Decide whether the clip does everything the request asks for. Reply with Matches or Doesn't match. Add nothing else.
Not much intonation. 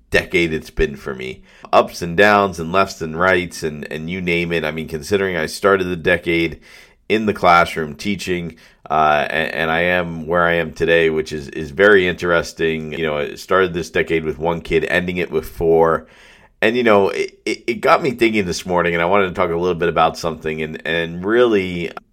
Matches